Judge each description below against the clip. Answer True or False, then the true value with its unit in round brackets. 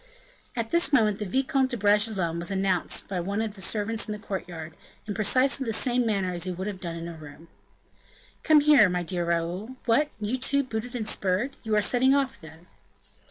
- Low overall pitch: False (210 Hz)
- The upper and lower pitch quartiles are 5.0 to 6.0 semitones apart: True (5.3 semitones)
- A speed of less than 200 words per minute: False (205 wpm)